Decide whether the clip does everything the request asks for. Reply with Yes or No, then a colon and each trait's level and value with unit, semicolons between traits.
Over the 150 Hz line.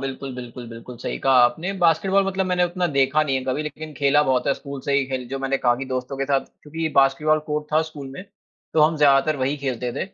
No: medium, 140 Hz